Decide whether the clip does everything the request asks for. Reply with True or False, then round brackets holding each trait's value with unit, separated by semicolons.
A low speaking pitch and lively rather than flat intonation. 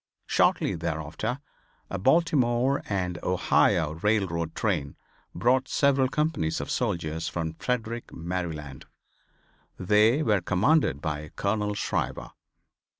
True (95 Hz; 7.0 semitones)